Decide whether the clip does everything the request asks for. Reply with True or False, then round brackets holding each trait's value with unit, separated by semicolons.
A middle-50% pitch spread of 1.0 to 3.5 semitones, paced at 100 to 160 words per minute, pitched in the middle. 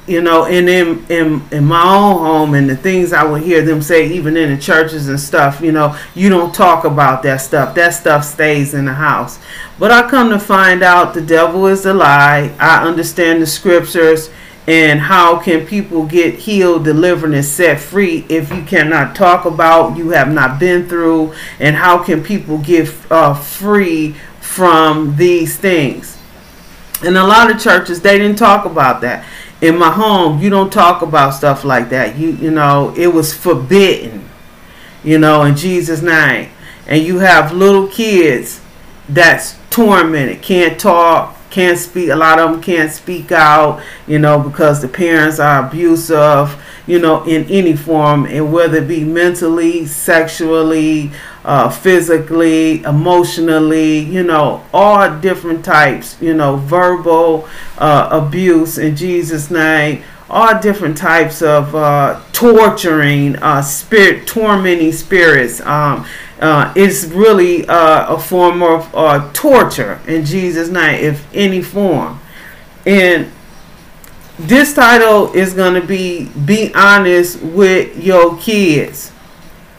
True (2.7 semitones; 150 wpm; 165 Hz)